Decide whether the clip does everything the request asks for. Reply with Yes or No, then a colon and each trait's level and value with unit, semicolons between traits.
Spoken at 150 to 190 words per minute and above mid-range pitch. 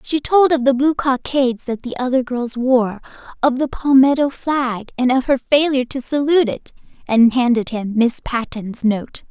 Yes: average, 180 wpm; very high, 255 Hz